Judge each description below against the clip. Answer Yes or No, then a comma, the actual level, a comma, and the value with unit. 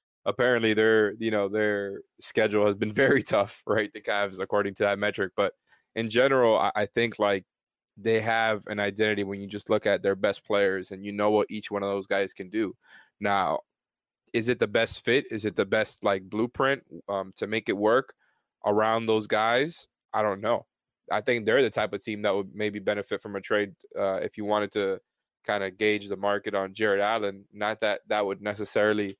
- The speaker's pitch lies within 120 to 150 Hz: No, low, 105 Hz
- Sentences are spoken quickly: Yes, fast, 210 wpm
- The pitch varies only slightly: Yes, narrow, 1.4 semitones